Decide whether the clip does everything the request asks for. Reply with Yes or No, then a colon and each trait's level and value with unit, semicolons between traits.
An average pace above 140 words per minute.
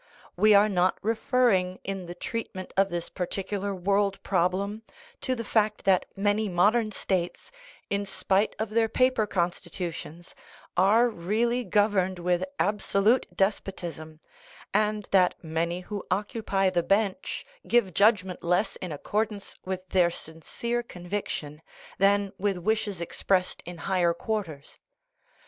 No: slow, 135 wpm